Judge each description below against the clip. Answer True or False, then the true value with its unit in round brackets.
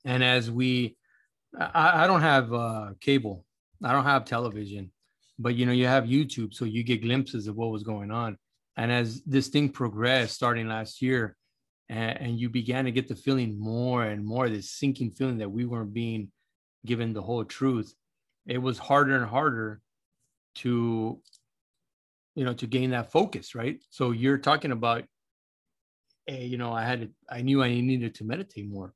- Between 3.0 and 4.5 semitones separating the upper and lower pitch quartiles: False (2.6 semitones)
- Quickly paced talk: False (180 wpm)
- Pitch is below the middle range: True (120 Hz)